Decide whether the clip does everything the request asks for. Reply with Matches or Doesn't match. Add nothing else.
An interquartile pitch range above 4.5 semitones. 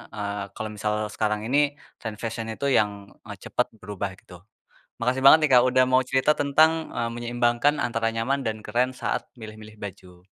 Doesn't match